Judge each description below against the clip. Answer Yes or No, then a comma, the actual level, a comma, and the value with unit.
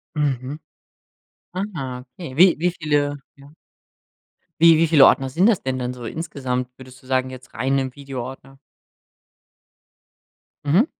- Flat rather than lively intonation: No, average, 3.6 semitones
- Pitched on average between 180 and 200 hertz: No, low, 135 Hz